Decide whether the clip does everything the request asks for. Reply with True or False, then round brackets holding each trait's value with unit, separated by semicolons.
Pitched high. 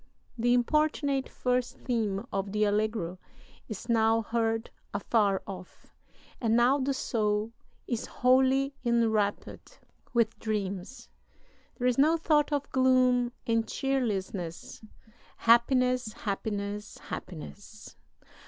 True (230 Hz)